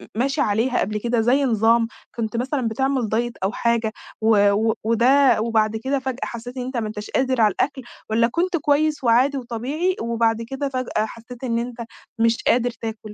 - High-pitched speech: Yes, high, 235 Hz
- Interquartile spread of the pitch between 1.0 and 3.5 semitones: Yes, average, 2.8 semitones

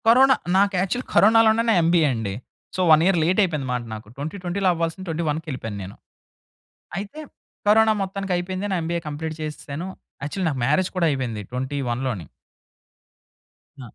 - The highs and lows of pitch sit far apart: Yes, wide, 5.8 semitones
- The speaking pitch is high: No, medium, 165 Hz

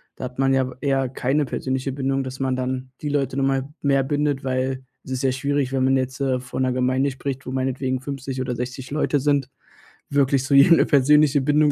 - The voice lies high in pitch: No, low, 135 Hz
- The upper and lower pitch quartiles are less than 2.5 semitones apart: Yes, narrow, 1.4 semitones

